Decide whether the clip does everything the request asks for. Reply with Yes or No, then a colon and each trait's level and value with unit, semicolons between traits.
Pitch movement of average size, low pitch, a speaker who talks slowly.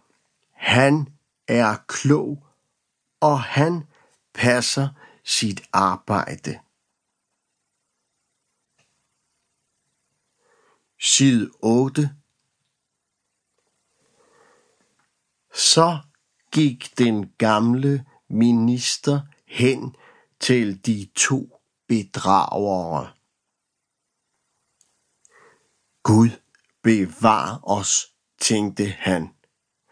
Yes: average, 3.9 semitones; low, 125 Hz; slow, 50 wpm